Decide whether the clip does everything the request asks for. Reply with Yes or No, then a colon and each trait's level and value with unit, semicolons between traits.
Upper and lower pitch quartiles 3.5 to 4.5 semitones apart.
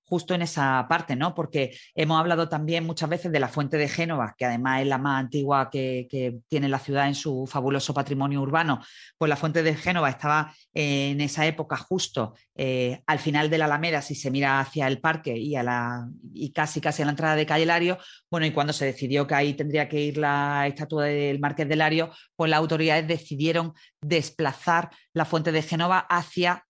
No: average, 2.7 semitones